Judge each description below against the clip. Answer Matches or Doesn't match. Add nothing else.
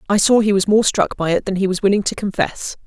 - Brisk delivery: Matches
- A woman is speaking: Matches